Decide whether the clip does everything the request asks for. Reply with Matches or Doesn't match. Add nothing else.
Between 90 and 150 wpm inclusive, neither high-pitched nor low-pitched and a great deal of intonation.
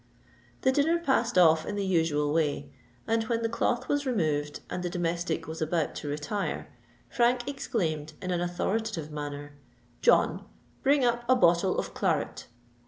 Doesn't match